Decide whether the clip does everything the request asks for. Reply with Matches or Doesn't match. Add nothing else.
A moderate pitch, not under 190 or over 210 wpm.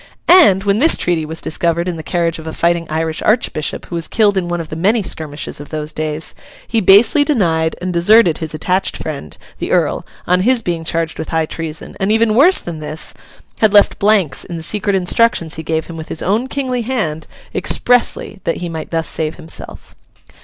Matches